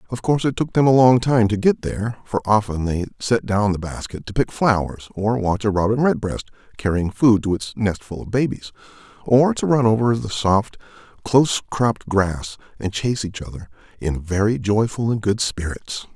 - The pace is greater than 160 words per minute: Yes, average, 195 wpm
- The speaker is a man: Yes, male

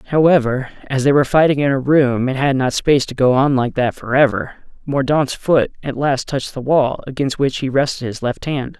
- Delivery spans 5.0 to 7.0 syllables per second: Yes, 5.2 syllables/s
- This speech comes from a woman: No, male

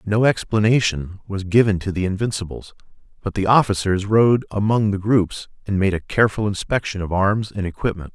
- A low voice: Yes, low, 100 Hz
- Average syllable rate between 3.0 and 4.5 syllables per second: No, 5.4 syllables/s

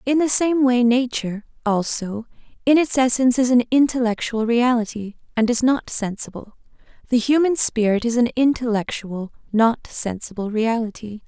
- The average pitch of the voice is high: Yes, high, 240 Hz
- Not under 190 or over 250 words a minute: No, average, 140 wpm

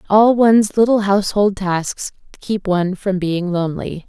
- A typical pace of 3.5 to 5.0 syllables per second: Yes, 4.7 syllables/s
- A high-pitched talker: Yes, high, 195 Hz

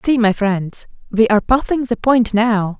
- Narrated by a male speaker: No, female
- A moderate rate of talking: Yes, average, 195 wpm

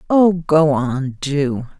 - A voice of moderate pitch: Yes, medium, 150 Hz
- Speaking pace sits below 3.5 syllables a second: Yes, 2.7 syllables/s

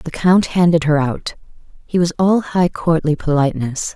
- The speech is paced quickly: No, average, 165 wpm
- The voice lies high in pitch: No, medium, 165 Hz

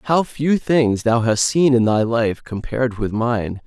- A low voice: Yes, low, 120 Hz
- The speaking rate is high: No, average, 195 wpm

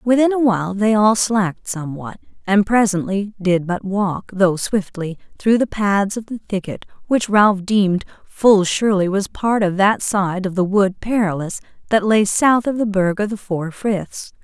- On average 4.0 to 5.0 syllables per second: Yes, 4.5 syllables/s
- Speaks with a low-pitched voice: No, high, 200 Hz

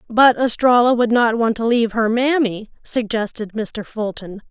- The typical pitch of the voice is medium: No, high, 230 Hz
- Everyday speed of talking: Yes, average, 160 wpm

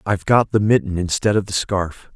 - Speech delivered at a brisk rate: Yes, fast, 225 wpm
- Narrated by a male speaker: Yes, male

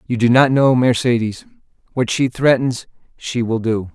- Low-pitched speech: Yes, low, 120 Hz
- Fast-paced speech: No, average, 165 wpm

